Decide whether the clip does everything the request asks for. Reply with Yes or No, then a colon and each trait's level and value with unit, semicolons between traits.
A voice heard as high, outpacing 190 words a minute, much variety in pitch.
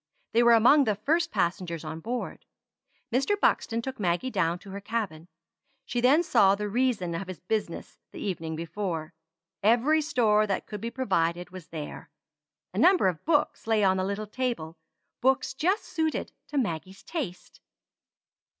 No: high, 210 Hz; average, 160 wpm; wide, 6.2 semitones